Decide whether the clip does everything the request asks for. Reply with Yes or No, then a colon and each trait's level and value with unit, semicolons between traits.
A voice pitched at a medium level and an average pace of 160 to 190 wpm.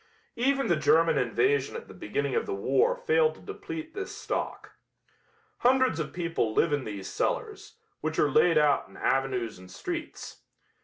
Yes: medium, 175 Hz; average, 165 wpm